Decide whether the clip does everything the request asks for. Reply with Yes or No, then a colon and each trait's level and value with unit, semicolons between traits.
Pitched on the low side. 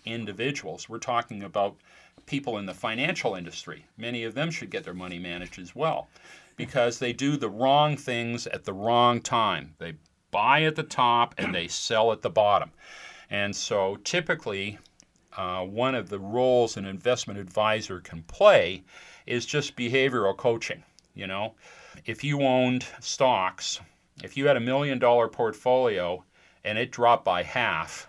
Yes: low, 120 Hz